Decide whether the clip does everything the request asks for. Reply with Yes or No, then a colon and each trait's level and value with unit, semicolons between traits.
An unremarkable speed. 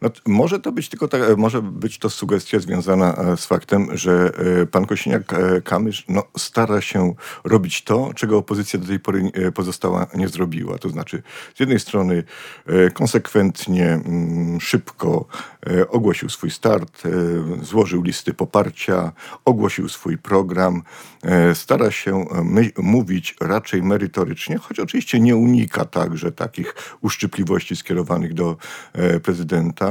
Yes: average, 120 wpm